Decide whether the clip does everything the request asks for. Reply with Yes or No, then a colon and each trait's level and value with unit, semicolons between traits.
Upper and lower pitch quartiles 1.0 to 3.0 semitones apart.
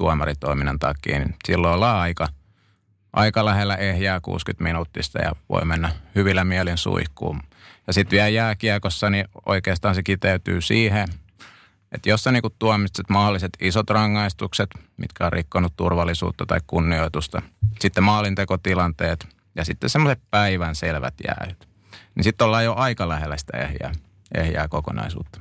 No: average, 3.7 semitones